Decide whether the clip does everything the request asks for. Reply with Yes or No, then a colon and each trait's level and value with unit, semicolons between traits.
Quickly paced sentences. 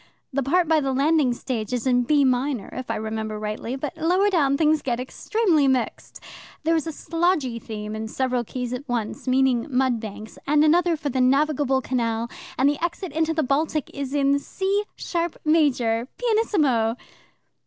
No: average, 175 wpm